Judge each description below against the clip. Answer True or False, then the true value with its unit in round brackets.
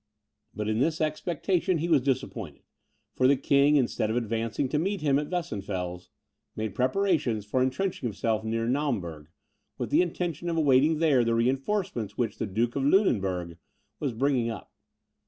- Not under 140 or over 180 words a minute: True (160 wpm)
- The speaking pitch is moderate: False (130 Hz)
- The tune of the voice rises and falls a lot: True (5.8 semitones)